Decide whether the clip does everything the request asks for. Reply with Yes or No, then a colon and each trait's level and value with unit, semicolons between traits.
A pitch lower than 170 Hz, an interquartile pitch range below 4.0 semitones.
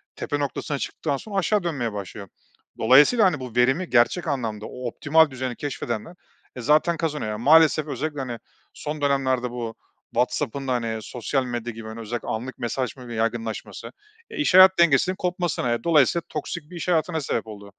No: low, 135 Hz; average, 5.1 semitones